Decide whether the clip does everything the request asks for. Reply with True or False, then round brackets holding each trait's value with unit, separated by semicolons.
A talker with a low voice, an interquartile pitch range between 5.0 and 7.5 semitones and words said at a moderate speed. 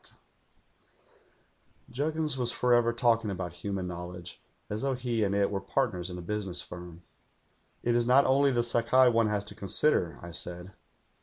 True (105 Hz; 5.3 semitones; 180 wpm)